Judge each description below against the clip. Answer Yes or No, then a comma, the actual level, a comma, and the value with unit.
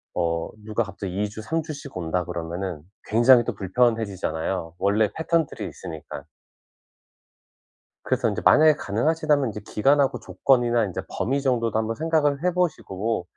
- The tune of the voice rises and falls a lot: Yes, wide, 6.6 semitones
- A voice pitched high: No, low, 110 Hz